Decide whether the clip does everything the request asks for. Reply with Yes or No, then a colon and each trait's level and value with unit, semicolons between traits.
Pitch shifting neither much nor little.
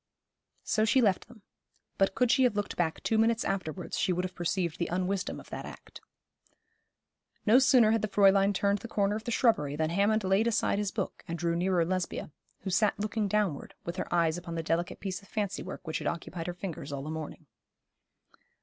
Yes: average, 3.7 semitones